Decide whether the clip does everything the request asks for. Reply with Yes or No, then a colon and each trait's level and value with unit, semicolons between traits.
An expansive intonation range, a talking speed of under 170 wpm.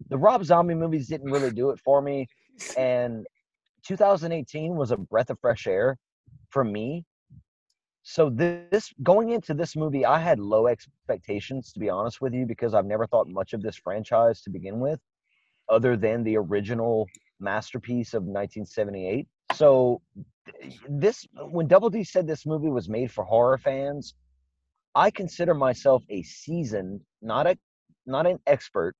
Yes: wide, 6.5 semitones; average, 155 wpm